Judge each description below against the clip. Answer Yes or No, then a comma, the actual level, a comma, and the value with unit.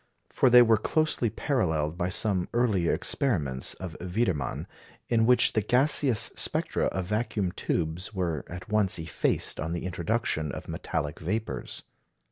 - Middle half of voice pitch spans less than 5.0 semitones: No, average, 5.3 semitones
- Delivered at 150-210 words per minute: No, average, 140 wpm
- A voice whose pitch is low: Yes, very low, 95 Hz